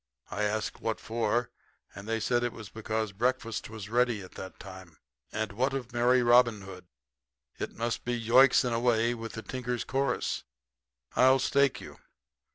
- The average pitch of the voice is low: Yes, low, 115 Hz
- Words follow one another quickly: No, average, 160 wpm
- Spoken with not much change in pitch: Yes, narrow, 2.3 semitones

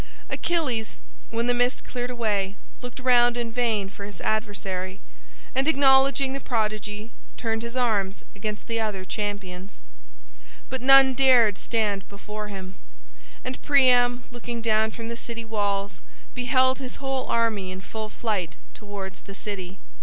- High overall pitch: Yes, high, 225 Hz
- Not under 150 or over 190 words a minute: No, average, 140 wpm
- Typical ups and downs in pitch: Yes, average, 3.5 semitones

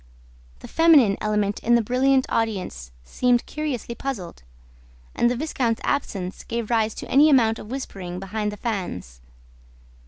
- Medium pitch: No, high, 225 Hz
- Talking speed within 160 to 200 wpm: No, average, 145 wpm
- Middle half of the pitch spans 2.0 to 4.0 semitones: No, average, 4.5 semitones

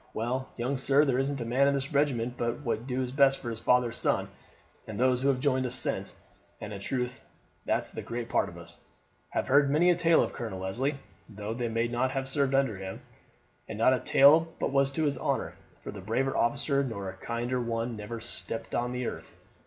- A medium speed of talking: No, fast, 220 wpm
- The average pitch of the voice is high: No, low, 125 Hz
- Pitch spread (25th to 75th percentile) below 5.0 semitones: Yes, average, 3.0 semitones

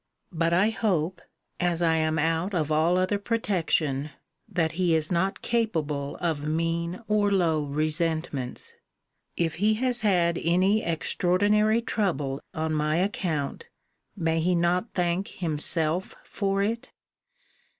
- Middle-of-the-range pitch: Yes, medium, 170 Hz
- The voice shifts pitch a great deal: No, average, 3.6 semitones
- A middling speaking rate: No, slow, 130 wpm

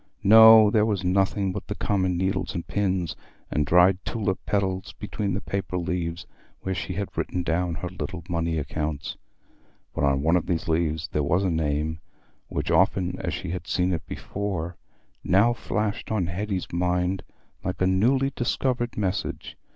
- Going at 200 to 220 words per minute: No, average, 165 wpm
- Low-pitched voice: Yes, very low, 90 Hz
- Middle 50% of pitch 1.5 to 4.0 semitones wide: Yes, average, 2.9 semitones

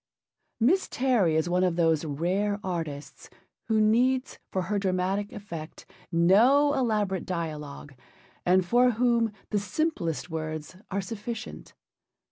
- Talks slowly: Yes, slow, 120 wpm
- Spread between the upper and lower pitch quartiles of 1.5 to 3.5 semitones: No, average, 5.3 semitones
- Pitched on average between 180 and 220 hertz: Yes, high, 190 Hz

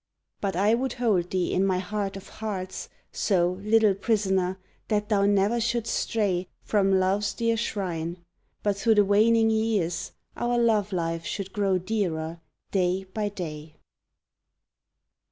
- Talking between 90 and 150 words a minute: Yes, average, 140 wpm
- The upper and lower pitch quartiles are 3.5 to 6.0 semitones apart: No, average, 3.0 semitones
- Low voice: No, high, 200 Hz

